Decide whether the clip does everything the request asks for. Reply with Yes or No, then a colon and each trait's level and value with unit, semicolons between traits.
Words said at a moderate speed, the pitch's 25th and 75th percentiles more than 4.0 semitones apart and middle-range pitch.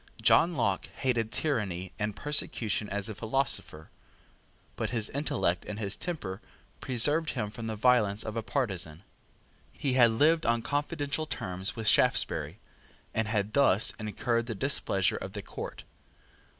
No: average, 145 wpm; average, 4.8 semitones; low, 115 Hz